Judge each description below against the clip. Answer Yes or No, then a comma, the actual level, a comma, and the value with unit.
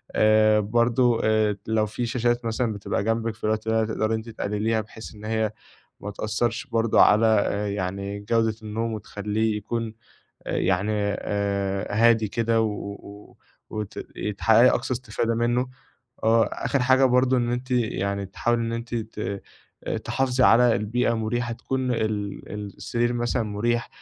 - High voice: No, low, 110 Hz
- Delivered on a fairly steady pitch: Yes, narrow, 2.1 semitones